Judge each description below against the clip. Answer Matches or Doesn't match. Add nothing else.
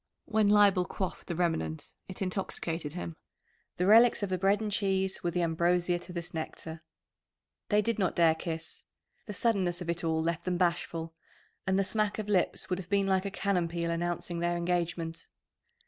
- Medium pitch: Matches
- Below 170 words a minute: Doesn't match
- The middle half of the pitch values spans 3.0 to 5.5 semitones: Doesn't match